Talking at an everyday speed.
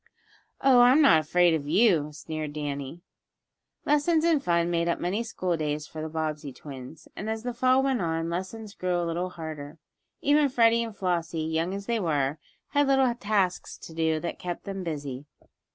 Yes: average, 185 wpm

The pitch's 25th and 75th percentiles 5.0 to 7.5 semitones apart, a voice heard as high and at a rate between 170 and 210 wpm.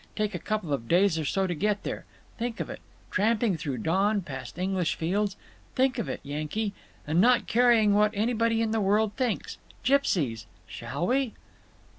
Yes: wide, 5.5 semitones; high, 205 Hz; average, 175 wpm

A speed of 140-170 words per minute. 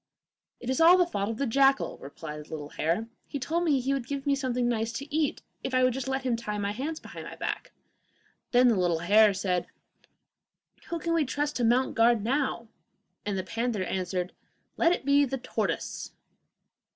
No: average, 200 wpm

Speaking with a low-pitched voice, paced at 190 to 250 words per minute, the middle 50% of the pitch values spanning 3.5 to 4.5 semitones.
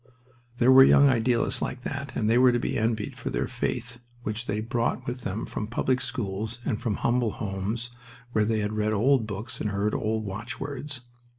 No: low, 115 Hz; average, 195 wpm; average, 2.7 semitones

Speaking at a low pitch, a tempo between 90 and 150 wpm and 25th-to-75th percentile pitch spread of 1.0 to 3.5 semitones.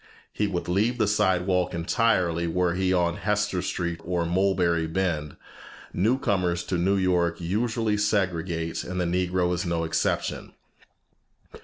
Yes: very low, 90 Hz; average, 140 wpm; narrow, 2.4 semitones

